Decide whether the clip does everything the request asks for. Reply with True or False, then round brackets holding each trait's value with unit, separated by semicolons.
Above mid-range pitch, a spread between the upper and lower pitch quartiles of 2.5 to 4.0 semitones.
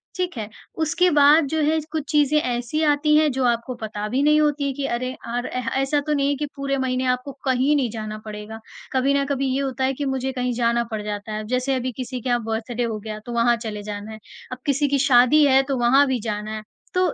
True (260 Hz; 3.4 semitones)